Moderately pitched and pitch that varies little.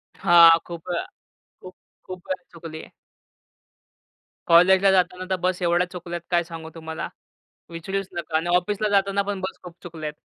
Yes: medium, 175 Hz; narrow, 2.0 semitones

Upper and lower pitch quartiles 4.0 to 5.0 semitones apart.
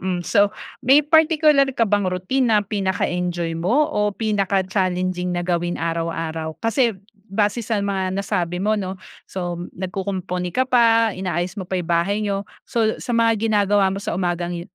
No: average, 3.6 semitones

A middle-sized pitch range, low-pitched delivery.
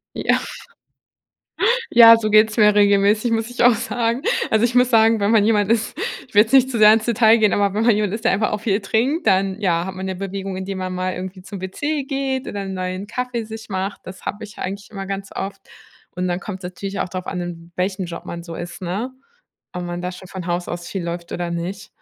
No: average, 3.2 semitones; high, 200 Hz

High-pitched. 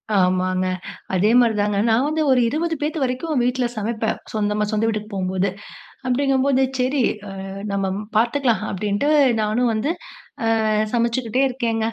Yes: high, 225 Hz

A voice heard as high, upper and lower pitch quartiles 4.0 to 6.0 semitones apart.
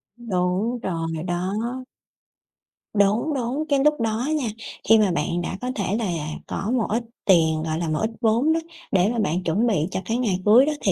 Yes: high, 210 Hz; average, 5.3 semitones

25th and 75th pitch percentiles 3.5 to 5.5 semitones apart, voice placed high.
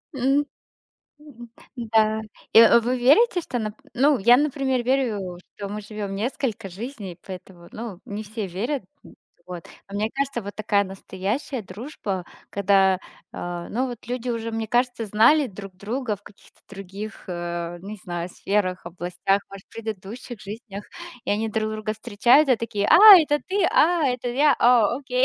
Yes: average, 4.1 semitones; high, 215 Hz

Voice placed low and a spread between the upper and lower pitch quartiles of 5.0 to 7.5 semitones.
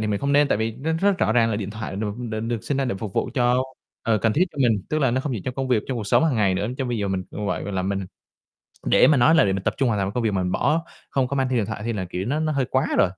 No: low, 115 Hz; average, 4.6 semitones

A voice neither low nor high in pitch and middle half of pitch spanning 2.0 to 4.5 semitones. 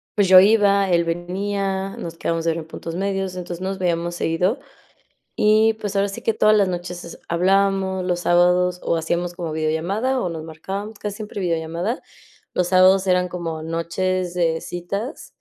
Yes: medium, 180 Hz; narrow, 2.5 semitones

